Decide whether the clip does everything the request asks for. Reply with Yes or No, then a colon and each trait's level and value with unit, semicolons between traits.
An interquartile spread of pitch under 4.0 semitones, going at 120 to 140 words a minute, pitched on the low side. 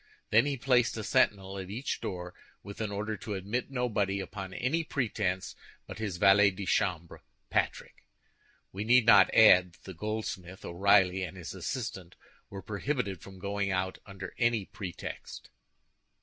No: average, 2.9 semitones; average, 155 wpm; low, 100 Hz